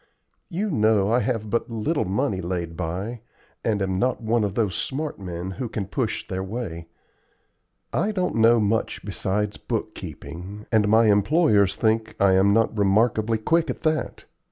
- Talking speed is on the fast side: No, average, 160 wpm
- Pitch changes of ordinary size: Yes, average, 3.7 semitones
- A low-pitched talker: Yes, low, 110 Hz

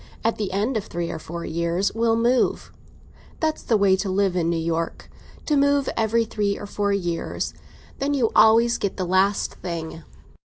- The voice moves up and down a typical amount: Yes, average, 4.8 semitones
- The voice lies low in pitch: No, high, 200 Hz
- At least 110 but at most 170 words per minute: No, average, 180 wpm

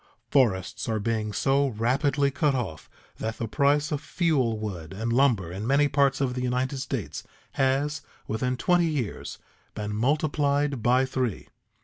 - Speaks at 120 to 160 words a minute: Yes, average, 150 wpm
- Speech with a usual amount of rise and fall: Yes, average, 4.2 semitones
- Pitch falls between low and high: No, low, 130 Hz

